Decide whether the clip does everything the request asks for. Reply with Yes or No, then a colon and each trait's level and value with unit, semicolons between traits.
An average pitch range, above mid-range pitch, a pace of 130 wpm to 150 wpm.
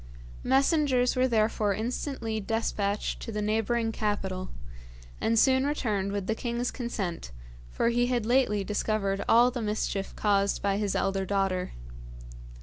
Yes: average, 3.3 semitones; high, 215 Hz; average, 140 wpm